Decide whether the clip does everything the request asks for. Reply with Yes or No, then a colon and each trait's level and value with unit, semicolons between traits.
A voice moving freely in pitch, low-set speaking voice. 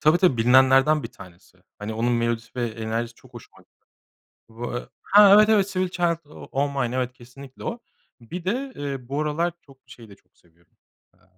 Yes: wide, 6.1 semitones; low, 130 Hz